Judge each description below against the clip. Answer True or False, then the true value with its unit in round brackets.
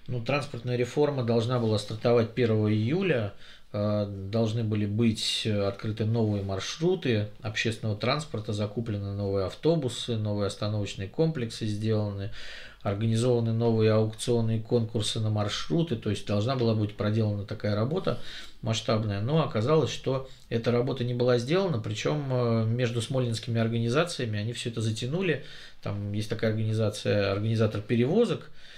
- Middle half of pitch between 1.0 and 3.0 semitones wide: True (2.6 semitones)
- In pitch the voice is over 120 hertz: False (115 Hz)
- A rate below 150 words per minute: True (125 wpm)